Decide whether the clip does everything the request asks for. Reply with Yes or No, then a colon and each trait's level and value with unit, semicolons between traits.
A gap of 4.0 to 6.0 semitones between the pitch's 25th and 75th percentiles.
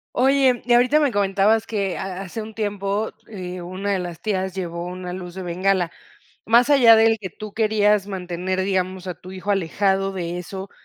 No: average, 2.9 semitones